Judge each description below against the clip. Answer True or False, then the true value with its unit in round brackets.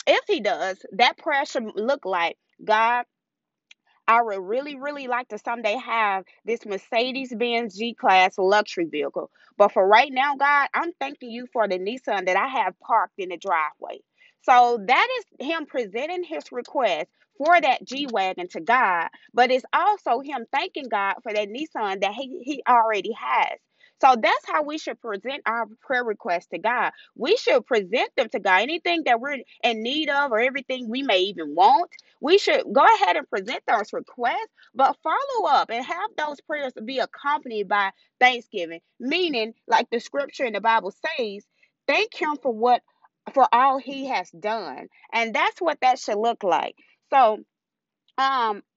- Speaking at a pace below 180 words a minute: True (170 wpm)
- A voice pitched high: True (245 Hz)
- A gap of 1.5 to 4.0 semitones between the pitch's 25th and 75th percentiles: False (5.2 semitones)